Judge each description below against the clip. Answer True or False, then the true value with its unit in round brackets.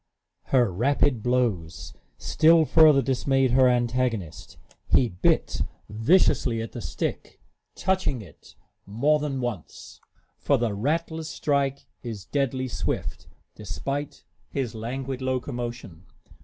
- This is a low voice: True (125 Hz)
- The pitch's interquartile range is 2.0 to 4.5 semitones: True (3.8 semitones)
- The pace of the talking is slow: True (110 wpm)